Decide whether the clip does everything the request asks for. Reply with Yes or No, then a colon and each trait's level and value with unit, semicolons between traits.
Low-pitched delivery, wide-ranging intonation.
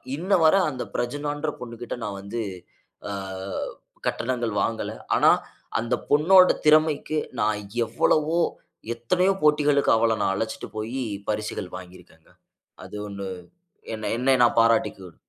Yes: low, 120 Hz; wide, 5.7 semitones